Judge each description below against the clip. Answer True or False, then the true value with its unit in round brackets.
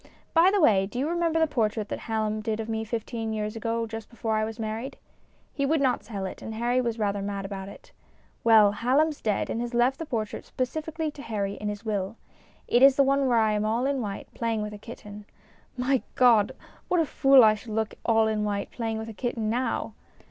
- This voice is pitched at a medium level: False (225 Hz)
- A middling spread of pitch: True (3.1 semitones)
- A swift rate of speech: True (230 wpm)